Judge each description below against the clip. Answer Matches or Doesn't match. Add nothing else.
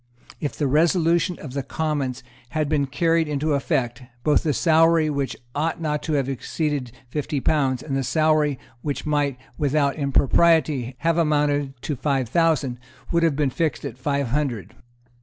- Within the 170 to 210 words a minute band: Doesn't match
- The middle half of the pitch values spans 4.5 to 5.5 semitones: Doesn't match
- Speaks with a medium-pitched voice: Matches